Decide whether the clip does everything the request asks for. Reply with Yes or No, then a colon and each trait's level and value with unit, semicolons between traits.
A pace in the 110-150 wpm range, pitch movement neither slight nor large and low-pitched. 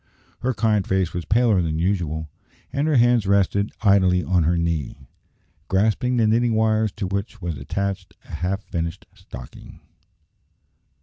Yes: average, 145 wpm; average, 4.2 semitones; low, 100 Hz